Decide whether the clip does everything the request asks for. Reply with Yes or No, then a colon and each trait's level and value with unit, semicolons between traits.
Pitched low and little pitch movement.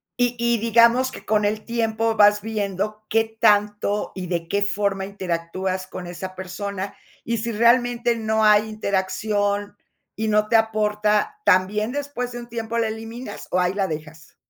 No: high, 210 Hz; narrow, 2.3 semitones